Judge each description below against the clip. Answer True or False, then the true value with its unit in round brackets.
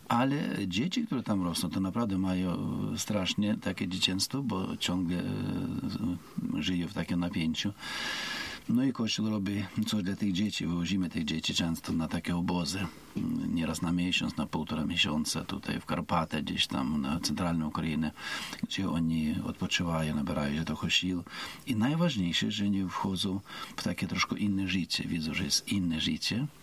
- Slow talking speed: False (155 wpm)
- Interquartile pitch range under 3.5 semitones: True (2.8 semitones)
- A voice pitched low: True (90 Hz)